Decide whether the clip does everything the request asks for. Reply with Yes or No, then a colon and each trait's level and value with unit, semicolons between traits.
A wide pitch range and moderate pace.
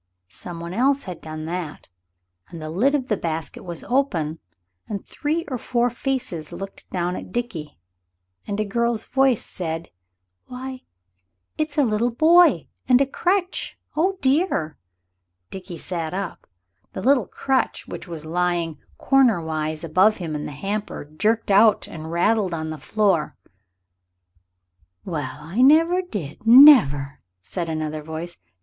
Yes: wide, 7.9 semitones; average, 145 wpm